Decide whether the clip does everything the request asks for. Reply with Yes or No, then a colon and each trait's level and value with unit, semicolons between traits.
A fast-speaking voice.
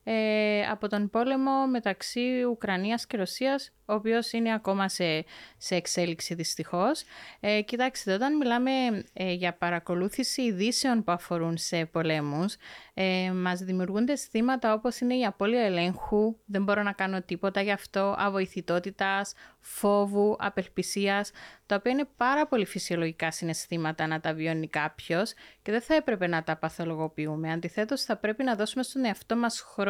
No: average, 150 wpm